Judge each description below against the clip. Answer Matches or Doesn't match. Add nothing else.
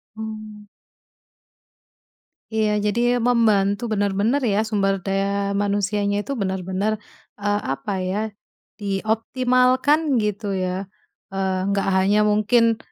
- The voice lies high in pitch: Matches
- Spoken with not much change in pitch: Matches